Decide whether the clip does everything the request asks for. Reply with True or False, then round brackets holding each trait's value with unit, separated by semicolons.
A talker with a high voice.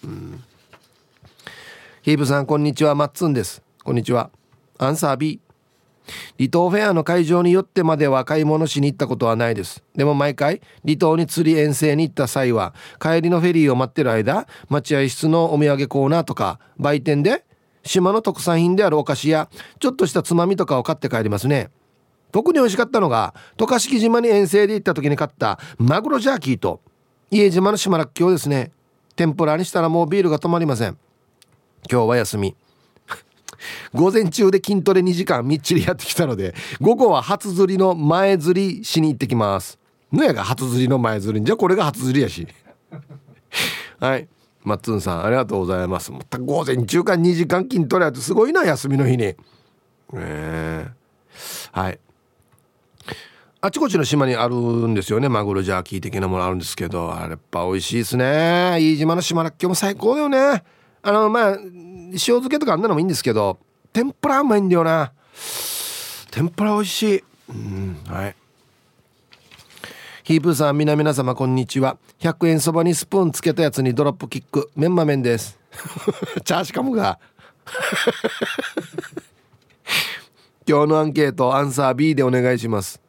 False (150 Hz)